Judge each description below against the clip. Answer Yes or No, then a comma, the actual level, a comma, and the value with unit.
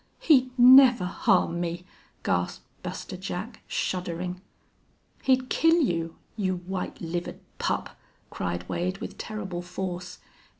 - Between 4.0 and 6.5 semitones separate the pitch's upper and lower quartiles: Yes, average, 5.1 semitones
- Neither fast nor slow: No, slow, 115 wpm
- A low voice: No, medium, 185 Hz